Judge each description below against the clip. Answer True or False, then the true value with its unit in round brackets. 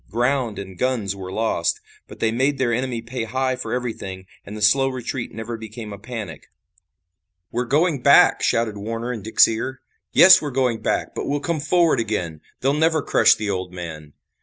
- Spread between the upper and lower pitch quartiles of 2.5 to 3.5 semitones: False (3.9 semitones)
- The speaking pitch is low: True (115 Hz)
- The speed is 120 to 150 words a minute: False (185 wpm)